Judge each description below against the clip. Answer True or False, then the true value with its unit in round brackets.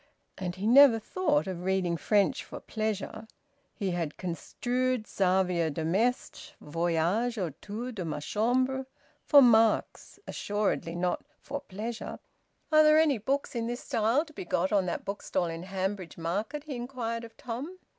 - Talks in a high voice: True (215 Hz)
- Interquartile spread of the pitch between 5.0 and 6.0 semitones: True (5.4 semitones)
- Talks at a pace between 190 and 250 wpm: False (155 wpm)